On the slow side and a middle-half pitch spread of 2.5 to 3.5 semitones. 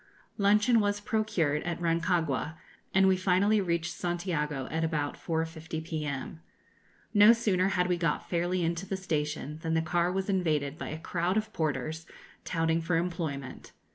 No: average, 155 wpm; average, 2.8 semitones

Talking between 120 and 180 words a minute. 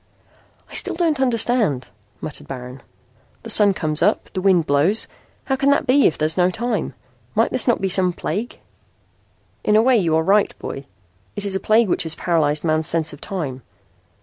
No: average, 195 wpm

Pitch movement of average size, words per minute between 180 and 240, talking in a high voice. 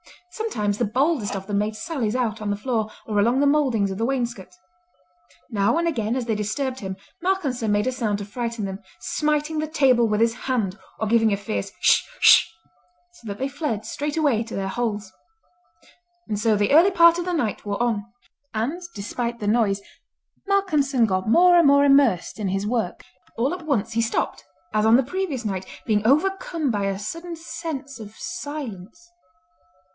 No: wide, 5.8 semitones; average, 185 wpm; high, 235 Hz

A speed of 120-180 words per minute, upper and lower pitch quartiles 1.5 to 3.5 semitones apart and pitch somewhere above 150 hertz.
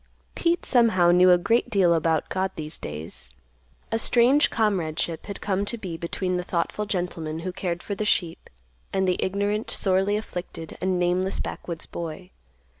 Yes: average, 165 wpm; average, 3.1 semitones; medium, 185 Hz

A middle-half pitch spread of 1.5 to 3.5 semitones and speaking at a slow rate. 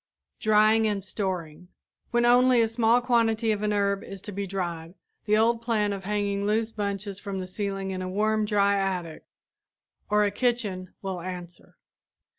No: narrow, 2.4 semitones; average, 170 wpm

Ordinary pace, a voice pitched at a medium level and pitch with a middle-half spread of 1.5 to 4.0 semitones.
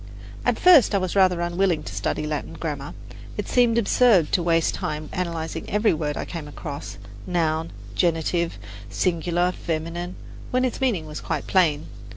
Yes: average, 160 wpm; medium, 170 Hz; average, 3.0 semitones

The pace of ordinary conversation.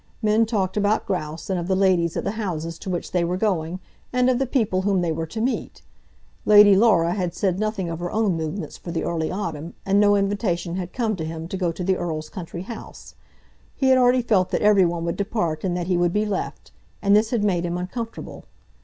No: fast, 235 wpm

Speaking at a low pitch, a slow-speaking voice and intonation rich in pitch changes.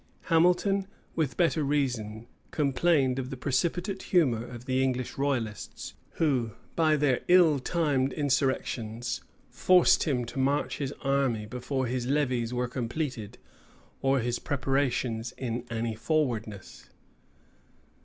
No: low, 130 Hz; slow, 120 wpm; average, 3.6 semitones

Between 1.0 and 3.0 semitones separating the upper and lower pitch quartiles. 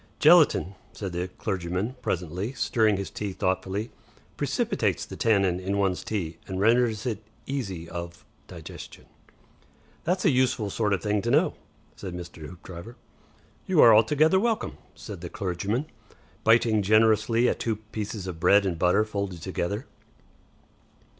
No: average, 3.7 semitones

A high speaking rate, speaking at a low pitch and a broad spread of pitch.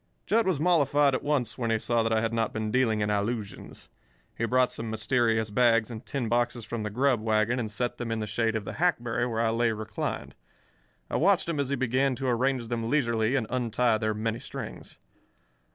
No: fast, 215 wpm; low, 115 Hz; narrow, 2.6 semitones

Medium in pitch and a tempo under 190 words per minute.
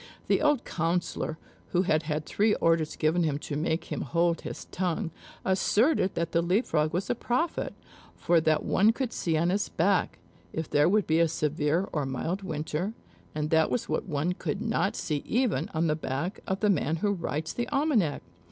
No: medium, 170 Hz; average, 195 wpm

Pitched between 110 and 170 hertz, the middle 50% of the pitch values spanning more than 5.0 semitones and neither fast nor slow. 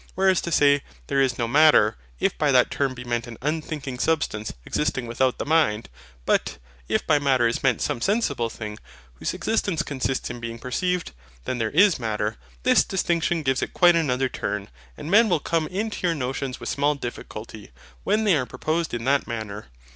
Yes: low, 135 Hz; wide, 5.6 semitones; average, 190 wpm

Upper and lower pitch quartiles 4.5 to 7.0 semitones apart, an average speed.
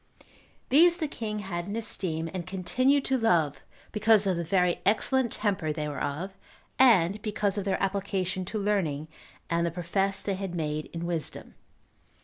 No: average, 3.8 semitones; average, 165 wpm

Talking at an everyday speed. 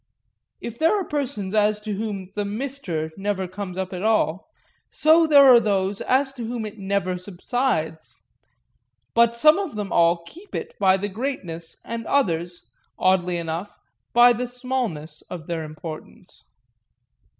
Yes: average, 150 wpm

